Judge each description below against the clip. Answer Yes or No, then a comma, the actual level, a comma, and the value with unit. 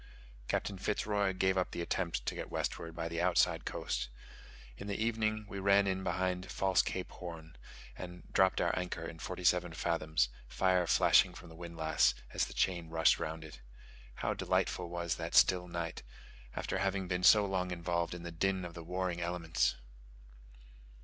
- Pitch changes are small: Yes, narrow, 2.1 semitones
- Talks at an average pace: Yes, average, 175 wpm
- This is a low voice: Yes, very low, 90 Hz